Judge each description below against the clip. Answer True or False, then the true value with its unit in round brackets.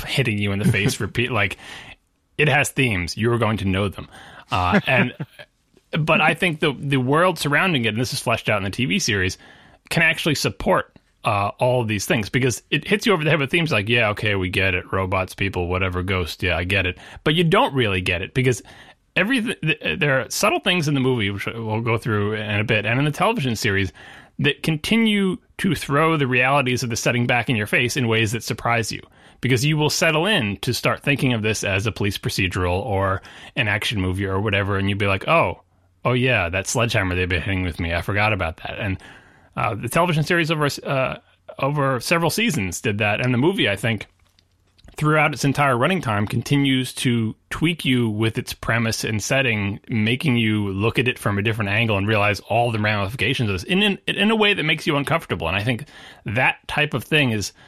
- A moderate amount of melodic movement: False (6.2 semitones)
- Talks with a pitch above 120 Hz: False (115 Hz)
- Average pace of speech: False (220 wpm)